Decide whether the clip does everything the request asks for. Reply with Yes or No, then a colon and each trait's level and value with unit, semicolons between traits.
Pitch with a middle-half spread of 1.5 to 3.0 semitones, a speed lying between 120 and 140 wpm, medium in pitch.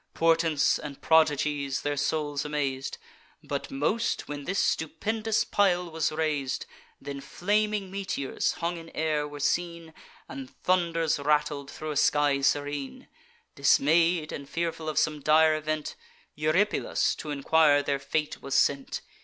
Yes: narrow, 2.5 semitones; slow, 135 wpm; medium, 155 Hz